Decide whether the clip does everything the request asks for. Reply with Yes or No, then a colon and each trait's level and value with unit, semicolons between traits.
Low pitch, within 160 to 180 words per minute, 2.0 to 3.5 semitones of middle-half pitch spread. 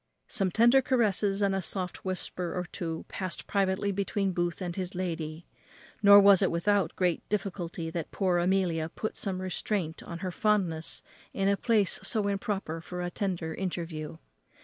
No: medium, 185 Hz; average, 165 wpm; average, 2.7 semitones